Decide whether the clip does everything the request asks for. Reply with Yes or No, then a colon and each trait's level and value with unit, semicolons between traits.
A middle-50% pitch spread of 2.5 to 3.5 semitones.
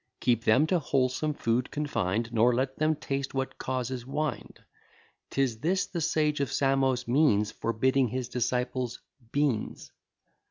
Yes: average, 3.2 semitones